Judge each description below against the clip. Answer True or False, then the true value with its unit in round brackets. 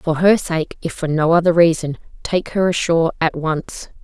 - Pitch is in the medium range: True (165 Hz)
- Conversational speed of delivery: True (195 wpm)